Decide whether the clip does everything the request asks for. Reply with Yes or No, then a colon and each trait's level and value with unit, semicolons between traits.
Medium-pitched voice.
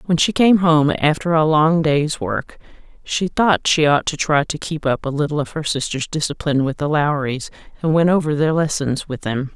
Yes: medium, 150 Hz